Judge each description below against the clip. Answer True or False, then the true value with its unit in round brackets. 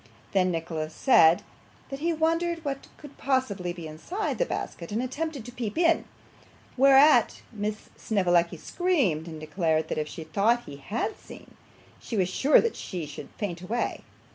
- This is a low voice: False (210 Hz)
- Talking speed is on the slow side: False (160 wpm)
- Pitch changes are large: True (8.4 semitones)